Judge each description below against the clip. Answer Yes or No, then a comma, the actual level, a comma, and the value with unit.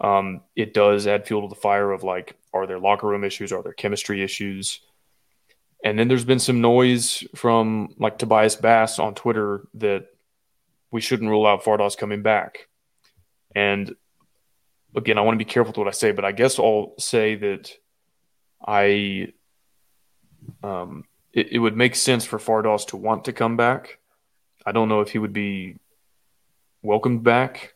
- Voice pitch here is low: Yes, low, 105 Hz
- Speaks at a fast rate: No, average, 170 wpm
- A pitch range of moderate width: No, narrow, 2.2 semitones